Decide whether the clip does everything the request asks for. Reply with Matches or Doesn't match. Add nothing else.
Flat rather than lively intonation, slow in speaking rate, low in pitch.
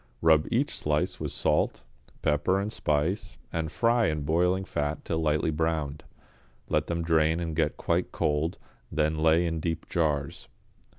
Doesn't match